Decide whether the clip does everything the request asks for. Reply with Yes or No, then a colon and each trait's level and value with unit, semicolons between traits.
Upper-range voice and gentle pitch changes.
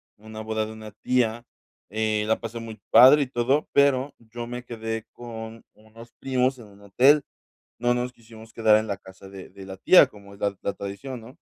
No: low, 110 Hz; narrow, 2.3 semitones